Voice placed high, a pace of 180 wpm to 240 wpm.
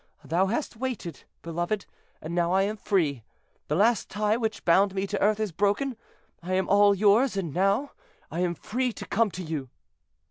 Yes: high, 195 Hz; average, 185 wpm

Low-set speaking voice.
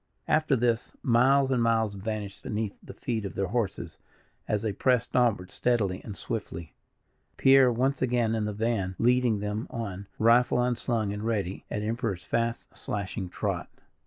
Yes: low, 115 Hz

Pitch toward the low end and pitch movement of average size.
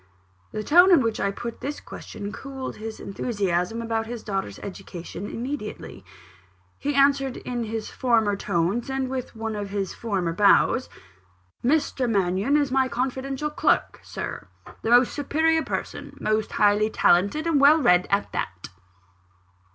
No: high, 230 Hz; average, 5.0 semitones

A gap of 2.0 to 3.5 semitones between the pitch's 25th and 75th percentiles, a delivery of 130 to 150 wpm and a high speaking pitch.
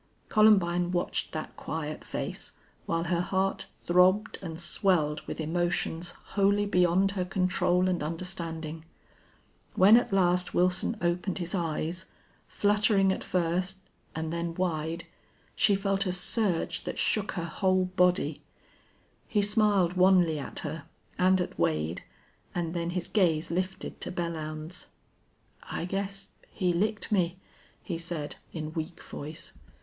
No: narrow, 2.4 semitones; slow, 135 wpm; medium, 180 Hz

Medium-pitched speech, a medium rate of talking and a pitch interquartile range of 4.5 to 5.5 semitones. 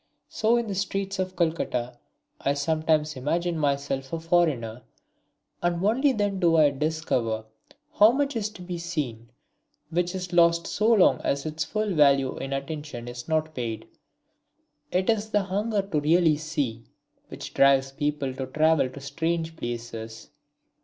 Yes: medium, 160 Hz; average, 155 wpm; average, 4.9 semitones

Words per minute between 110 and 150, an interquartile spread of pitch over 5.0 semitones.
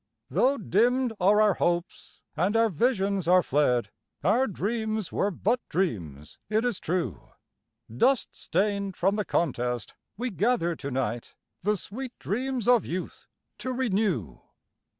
Yes: slow, 135 wpm; wide, 5.5 semitones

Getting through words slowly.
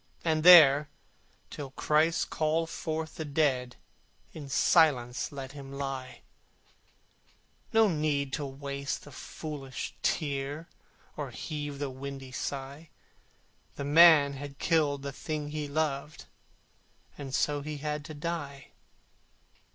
Yes: slow, 120 wpm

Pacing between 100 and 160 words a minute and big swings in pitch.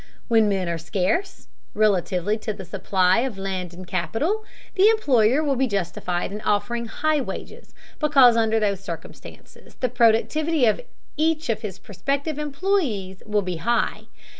Yes: average, 150 wpm; wide, 6.5 semitones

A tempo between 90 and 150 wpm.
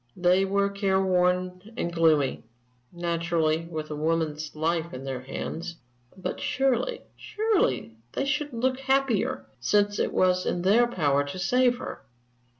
Yes: average, 145 wpm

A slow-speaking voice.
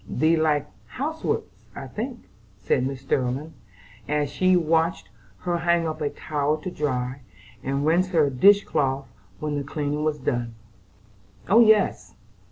No: average, 150 wpm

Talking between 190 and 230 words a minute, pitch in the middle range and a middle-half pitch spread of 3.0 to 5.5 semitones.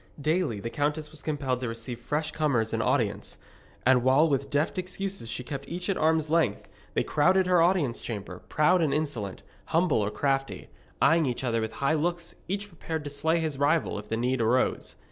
Yes: average, 195 wpm; medium, 145 Hz; average, 4.8 semitones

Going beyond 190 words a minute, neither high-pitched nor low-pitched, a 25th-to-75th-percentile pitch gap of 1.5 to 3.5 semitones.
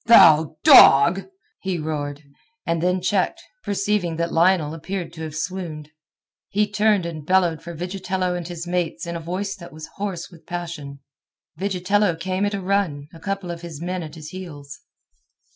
No: average, 170 wpm; medium, 175 Hz; average, 2.9 semitones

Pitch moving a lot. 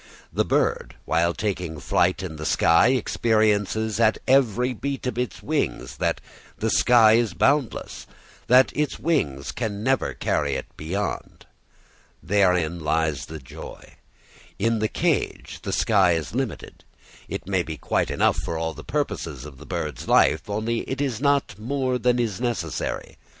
Yes: wide, 6.9 semitones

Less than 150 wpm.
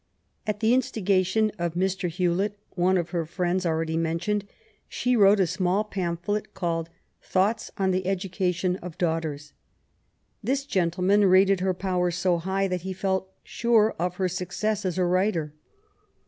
No: average, 155 wpm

